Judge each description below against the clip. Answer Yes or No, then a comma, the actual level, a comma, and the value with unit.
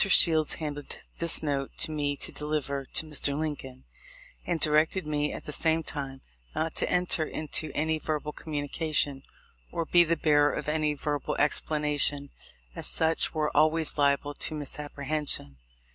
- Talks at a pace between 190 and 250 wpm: No, average, 150 wpm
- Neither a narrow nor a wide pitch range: No, narrow, 1.6 semitones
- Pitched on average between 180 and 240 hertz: No, medium, 150 Hz